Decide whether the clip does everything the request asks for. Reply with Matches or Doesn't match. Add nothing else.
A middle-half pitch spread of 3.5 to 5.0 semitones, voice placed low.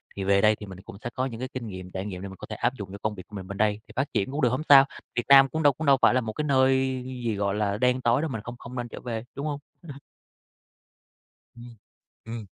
Matches